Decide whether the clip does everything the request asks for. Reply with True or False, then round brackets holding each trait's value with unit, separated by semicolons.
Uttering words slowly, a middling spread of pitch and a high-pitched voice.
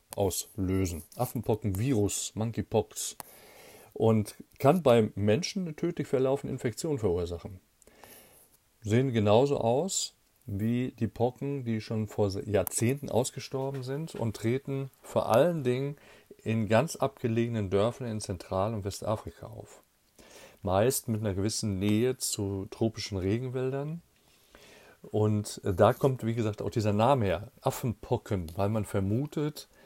False (120 wpm; 4.0 semitones; 110 Hz)